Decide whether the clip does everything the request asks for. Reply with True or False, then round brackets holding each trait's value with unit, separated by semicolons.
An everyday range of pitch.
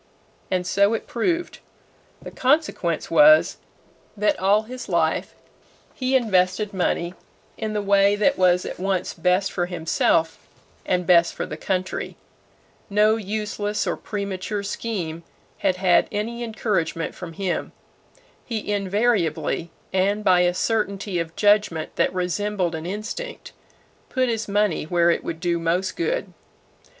True (3.2 semitones)